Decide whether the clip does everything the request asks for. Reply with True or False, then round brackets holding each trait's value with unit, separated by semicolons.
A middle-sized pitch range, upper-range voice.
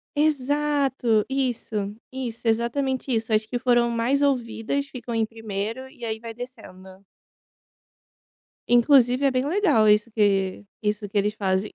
True (3.6 semitones; 235 Hz)